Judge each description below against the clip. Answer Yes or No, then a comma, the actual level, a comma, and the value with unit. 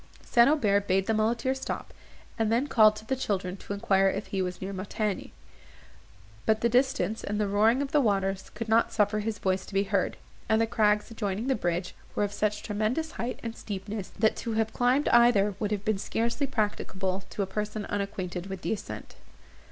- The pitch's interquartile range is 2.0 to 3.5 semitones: Yes, narrow, 2.5 semitones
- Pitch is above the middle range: Yes, high, 210 Hz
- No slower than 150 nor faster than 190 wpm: No, average, 200 wpm